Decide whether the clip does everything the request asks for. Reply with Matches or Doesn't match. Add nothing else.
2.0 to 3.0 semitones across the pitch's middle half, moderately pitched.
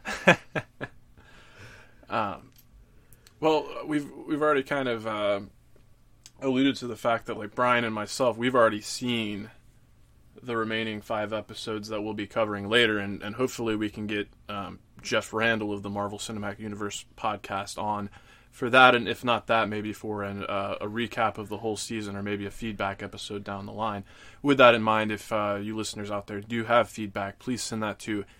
Doesn't match